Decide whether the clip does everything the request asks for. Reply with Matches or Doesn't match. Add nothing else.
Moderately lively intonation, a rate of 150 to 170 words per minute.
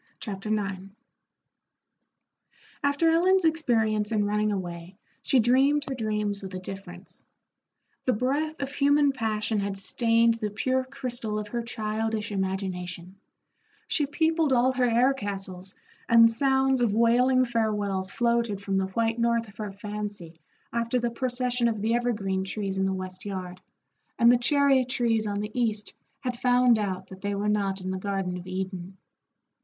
Matches